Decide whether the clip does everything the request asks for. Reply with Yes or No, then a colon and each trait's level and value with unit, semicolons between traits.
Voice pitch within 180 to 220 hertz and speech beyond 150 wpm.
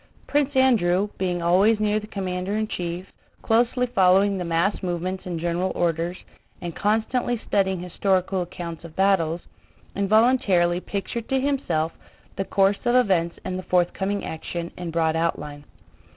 No: medium, 185 Hz; average, 145 wpm